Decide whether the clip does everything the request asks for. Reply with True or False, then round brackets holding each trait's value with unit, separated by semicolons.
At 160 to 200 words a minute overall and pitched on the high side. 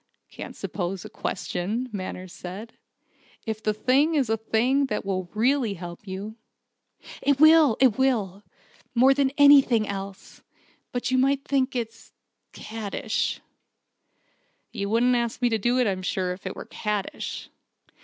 False (150 wpm; 225 Hz)